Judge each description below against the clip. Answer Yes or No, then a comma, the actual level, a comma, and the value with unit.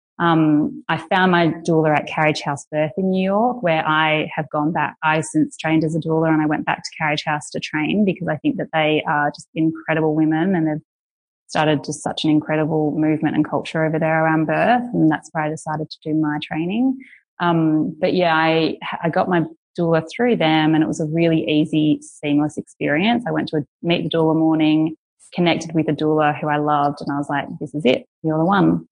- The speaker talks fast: Yes, fast, 220 wpm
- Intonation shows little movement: Yes, narrow, 1.1 semitones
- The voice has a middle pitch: Yes, medium, 155 Hz